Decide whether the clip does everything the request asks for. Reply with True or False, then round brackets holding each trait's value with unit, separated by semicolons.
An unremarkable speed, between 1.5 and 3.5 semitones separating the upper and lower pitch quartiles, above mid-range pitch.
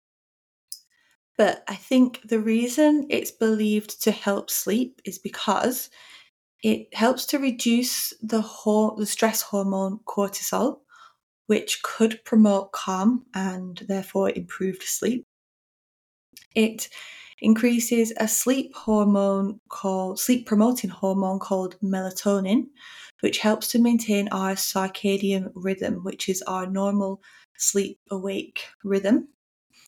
False (105 wpm; 3.2 semitones; 210 Hz)